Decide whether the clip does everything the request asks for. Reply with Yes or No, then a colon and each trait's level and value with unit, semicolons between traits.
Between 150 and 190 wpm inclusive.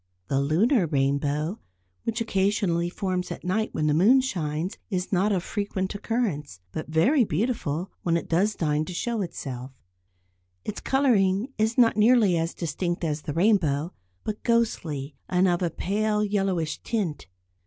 Yes: average, 155 wpm